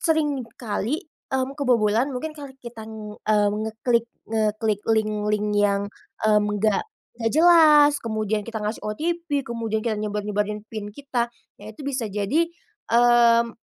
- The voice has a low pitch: No, high, 225 Hz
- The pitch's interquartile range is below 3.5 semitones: No, average, 4.3 semitones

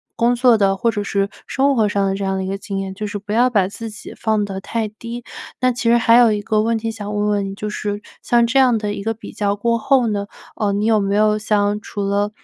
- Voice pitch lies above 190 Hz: Yes, high, 210 Hz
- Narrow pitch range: Yes, narrow, 2.3 semitones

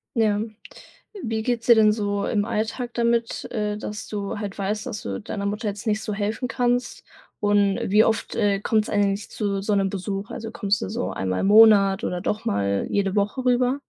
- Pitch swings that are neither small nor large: No, narrow, 2.0 semitones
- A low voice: No, high, 210 Hz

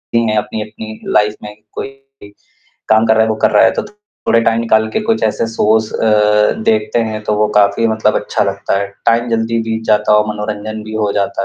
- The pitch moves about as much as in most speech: No, narrow, 1.0 semitones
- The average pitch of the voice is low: Yes, low, 110 Hz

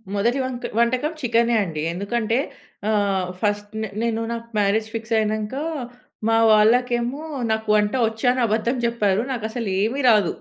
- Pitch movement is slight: Yes, narrow, 2.3 semitones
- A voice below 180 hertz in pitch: No, high, 225 Hz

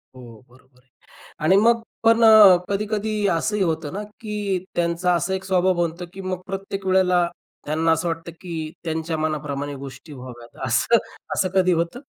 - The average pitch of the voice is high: No, medium, 175 Hz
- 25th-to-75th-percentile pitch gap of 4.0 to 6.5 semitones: No, average, 3.6 semitones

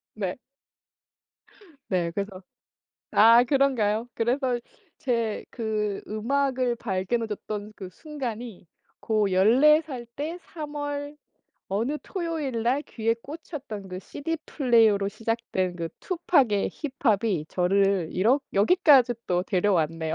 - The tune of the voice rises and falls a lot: Yes, wide, 5.7 semitones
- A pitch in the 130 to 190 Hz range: No, high, 230 Hz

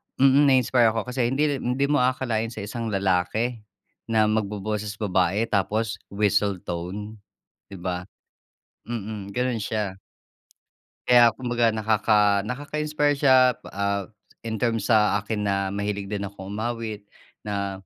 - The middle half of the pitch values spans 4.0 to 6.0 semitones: No, average, 3.3 semitones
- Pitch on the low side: Yes, low, 110 Hz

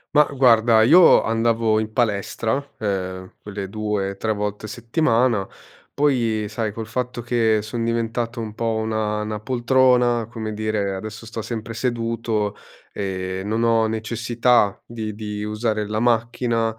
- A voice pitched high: No, low, 110 Hz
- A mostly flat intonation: Yes, narrow, 1.8 semitones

